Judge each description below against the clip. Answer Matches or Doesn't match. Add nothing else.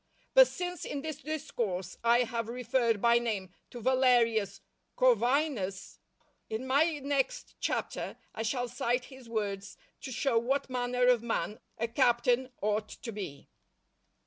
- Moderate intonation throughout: Matches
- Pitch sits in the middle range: Doesn't match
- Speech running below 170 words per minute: Matches